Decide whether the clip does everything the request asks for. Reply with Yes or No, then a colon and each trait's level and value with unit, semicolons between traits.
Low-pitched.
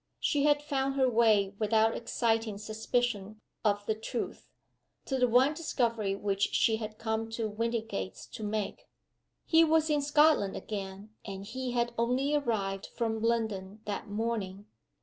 No: high, 225 Hz